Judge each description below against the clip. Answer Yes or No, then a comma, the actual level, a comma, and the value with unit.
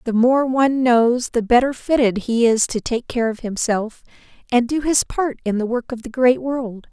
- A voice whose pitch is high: Yes, high, 240 Hz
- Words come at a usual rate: No, fast, 215 wpm